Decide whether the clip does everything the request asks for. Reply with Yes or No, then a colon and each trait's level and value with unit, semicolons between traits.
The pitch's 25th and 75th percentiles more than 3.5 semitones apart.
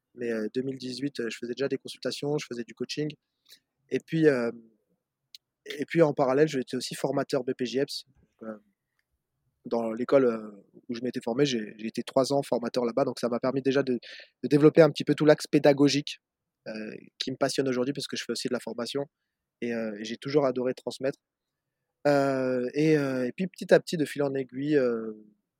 No: average, 3.1 semitones